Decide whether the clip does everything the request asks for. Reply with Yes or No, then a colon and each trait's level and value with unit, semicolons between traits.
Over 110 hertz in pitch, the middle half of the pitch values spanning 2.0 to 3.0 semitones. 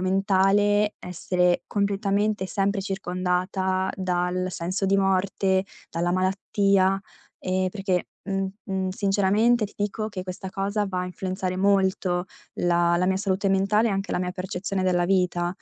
No: high, 190 Hz; narrow, 1.4 semitones